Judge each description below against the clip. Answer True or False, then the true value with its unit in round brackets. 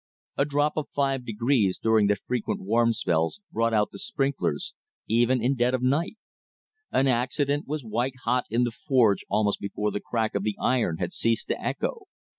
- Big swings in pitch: False (3.9 semitones)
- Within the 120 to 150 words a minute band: False (185 wpm)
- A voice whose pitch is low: True (120 Hz)